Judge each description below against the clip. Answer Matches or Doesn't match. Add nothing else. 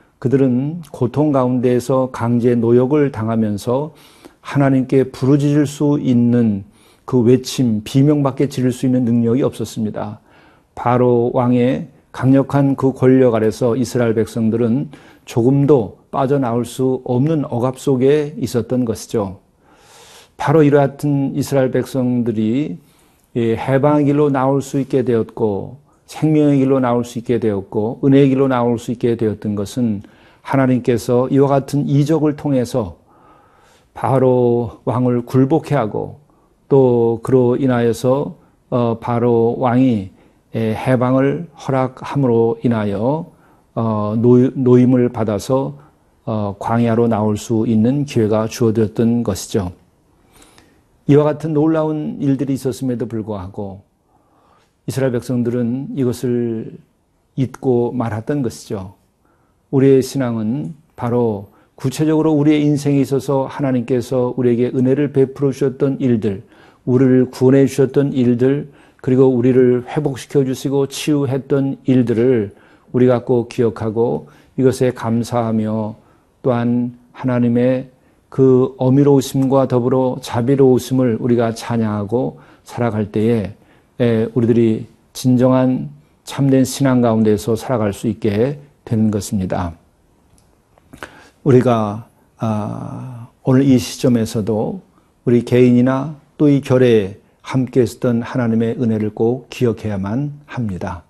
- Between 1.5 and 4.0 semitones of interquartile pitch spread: Matches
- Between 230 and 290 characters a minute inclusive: Matches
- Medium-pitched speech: Doesn't match